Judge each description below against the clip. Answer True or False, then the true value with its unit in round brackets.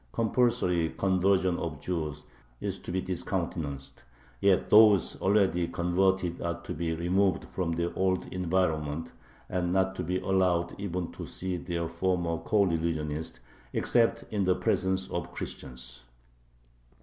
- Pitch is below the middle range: True (90 Hz)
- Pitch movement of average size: False (2.2 semitones)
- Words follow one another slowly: True (130 wpm)